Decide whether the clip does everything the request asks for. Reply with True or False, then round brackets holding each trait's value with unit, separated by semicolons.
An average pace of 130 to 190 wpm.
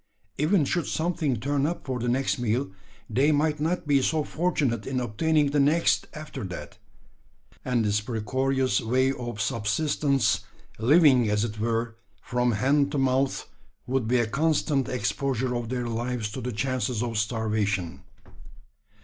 True (150 wpm)